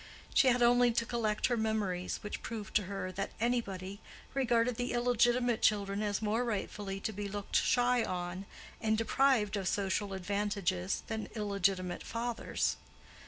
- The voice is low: No, high, 210 Hz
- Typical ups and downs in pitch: Yes, average, 3.2 semitones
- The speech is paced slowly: No, average, 150 wpm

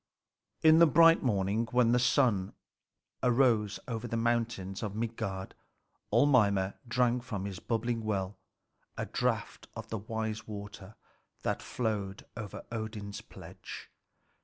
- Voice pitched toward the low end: Yes, low, 110 Hz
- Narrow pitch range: No, average, 3.1 semitones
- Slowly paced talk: Yes, slow, 130 wpm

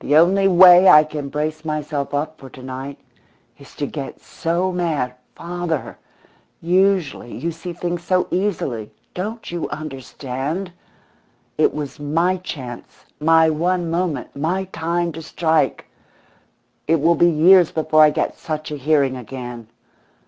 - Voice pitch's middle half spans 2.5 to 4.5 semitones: Yes, average, 3.4 semitones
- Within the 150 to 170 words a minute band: No, average, 140 wpm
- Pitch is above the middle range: No, medium, 160 Hz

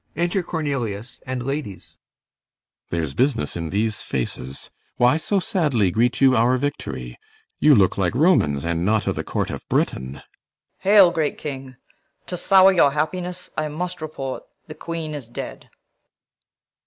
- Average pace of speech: Yes, average, 150 wpm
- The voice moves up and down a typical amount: No, wide, 7.7 semitones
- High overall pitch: No, low, 135 Hz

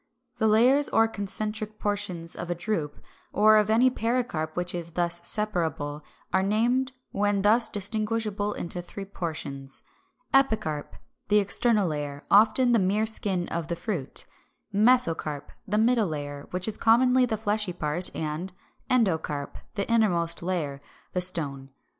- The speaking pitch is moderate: No, high, 200 Hz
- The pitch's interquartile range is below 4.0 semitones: No, average, 4.6 semitones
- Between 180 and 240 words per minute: No, average, 140 wpm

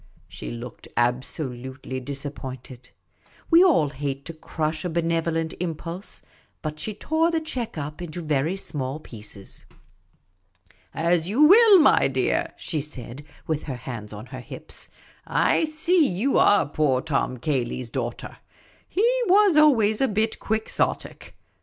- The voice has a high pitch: No, medium, 155 Hz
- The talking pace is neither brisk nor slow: Yes, average, 145 wpm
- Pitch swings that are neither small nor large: No, wide, 8.7 semitones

